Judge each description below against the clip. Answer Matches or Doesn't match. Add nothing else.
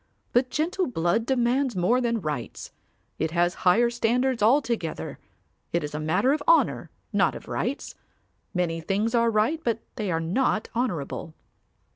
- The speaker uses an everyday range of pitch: Doesn't match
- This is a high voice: Matches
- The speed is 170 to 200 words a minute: Doesn't match